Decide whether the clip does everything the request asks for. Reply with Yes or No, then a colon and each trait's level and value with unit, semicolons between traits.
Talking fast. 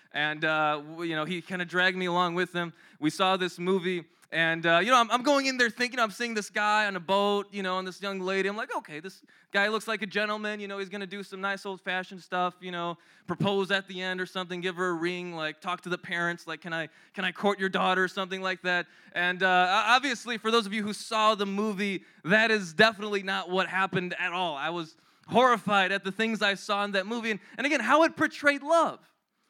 Yes: fast, 255 wpm